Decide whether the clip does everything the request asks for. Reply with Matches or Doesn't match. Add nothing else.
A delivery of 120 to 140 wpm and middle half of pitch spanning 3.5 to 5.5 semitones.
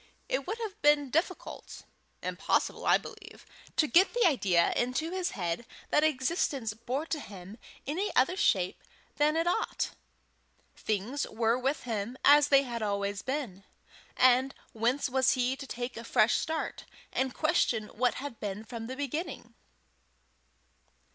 Doesn't match